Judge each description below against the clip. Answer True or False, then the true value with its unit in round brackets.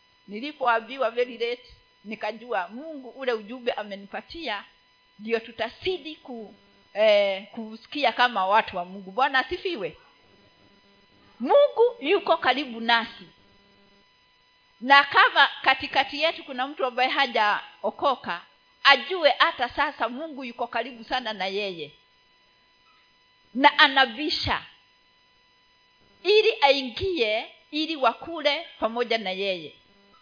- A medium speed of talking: False (95 wpm)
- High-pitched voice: True (250 Hz)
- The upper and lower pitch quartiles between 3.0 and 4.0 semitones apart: False (5.2 semitones)